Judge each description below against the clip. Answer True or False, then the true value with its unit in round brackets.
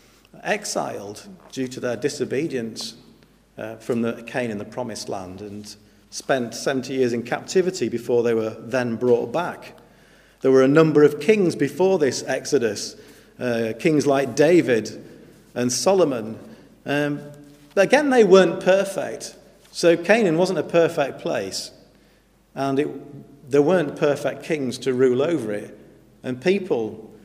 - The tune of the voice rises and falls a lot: True (5.9 semitones)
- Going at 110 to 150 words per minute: True (140 wpm)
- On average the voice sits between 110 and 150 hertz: True (140 Hz)